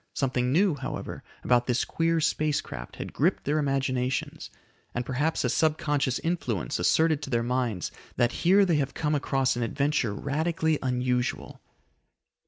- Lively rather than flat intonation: No, average, 3.8 semitones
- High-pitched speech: No, low, 135 Hz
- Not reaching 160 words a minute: Yes, average, 150 wpm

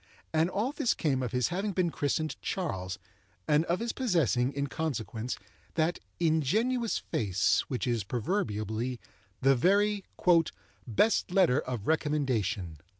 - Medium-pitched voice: Yes, medium, 150 Hz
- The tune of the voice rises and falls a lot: Yes, wide, 7.3 semitones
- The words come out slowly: Yes, slow, 130 wpm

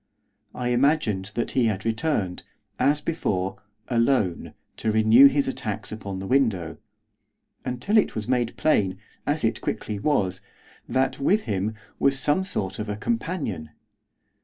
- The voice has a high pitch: No, low, 115 Hz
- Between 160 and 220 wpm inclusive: No, average, 140 wpm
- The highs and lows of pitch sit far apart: Yes, wide, 5.8 semitones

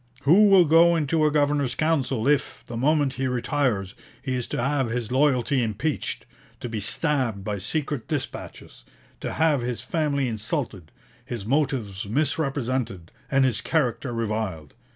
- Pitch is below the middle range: Yes, low, 130 Hz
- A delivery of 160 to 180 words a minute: No, average, 150 wpm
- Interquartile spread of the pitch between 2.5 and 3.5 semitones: No, average, 4.4 semitones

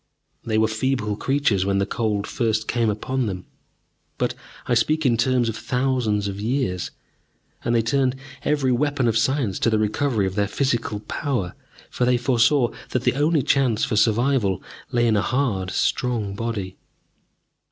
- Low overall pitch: Yes, low, 115 Hz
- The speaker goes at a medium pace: Yes, average, 165 wpm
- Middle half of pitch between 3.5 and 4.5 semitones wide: Yes, average, 3.9 semitones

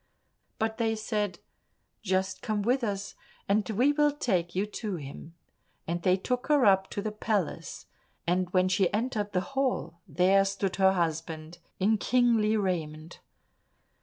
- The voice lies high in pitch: Yes, high, 195 Hz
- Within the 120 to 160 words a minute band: Yes, average, 150 wpm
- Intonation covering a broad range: No, average, 3.5 semitones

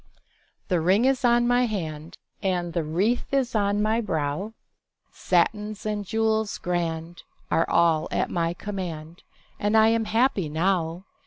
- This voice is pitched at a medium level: No, high, 195 Hz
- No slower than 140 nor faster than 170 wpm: Yes, average, 145 wpm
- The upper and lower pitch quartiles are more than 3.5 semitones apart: Yes, average, 4.7 semitones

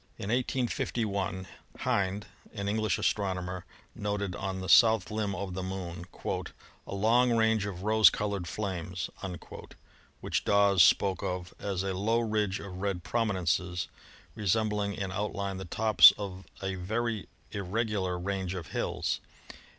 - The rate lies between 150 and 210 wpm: No, slow, 135 wpm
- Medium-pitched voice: No, low, 100 Hz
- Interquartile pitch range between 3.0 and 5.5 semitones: No, narrow, 2.5 semitones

